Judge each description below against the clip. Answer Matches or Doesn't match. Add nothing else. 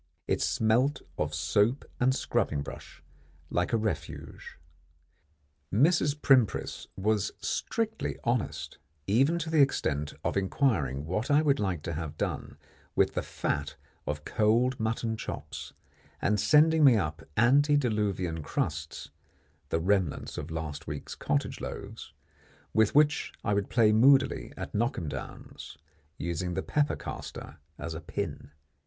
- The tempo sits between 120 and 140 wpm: Matches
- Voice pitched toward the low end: Matches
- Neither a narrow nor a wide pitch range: Doesn't match